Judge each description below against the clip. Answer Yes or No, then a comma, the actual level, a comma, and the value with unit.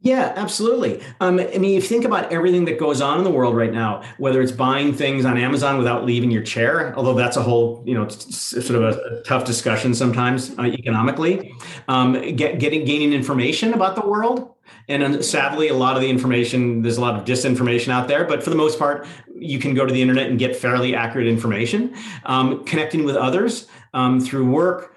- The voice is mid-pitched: No, low, 130 Hz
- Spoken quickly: Yes, fast, 210 wpm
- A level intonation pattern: No, average, 4.6 semitones